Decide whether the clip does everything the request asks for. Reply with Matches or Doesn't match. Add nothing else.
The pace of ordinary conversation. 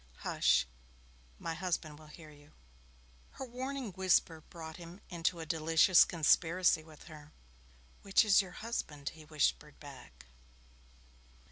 Doesn't match